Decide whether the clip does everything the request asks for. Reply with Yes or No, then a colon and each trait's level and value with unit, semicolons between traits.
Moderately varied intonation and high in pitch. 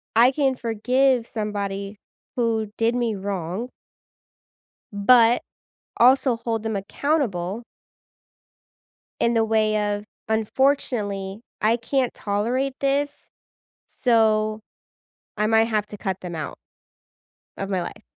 Yes: average, 3.2 semitones; high, 220 Hz